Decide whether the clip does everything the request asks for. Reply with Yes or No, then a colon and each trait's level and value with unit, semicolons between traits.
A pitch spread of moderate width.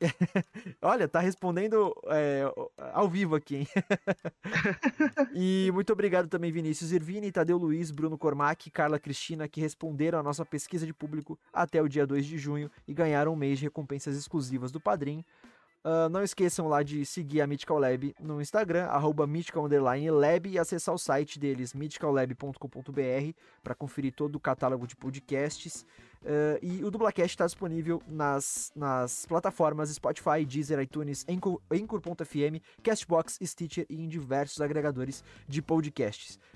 Yes: average, 3.2 semitones